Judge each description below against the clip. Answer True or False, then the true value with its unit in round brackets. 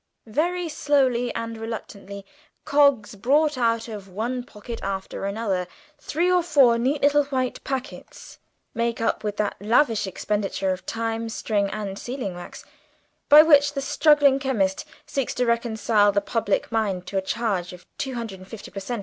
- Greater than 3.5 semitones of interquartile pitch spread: True (5.1 semitones)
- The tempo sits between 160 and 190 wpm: True (165 wpm)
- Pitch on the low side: False (230 Hz)